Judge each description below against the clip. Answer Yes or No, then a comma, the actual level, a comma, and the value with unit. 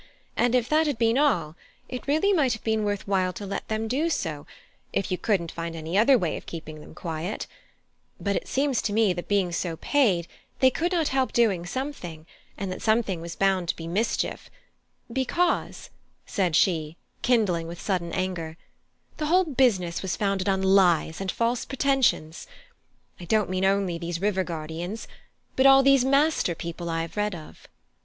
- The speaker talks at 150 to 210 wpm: Yes, average, 180 wpm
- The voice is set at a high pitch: Yes, high, 195 Hz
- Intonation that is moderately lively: No, wide, 6.6 semitones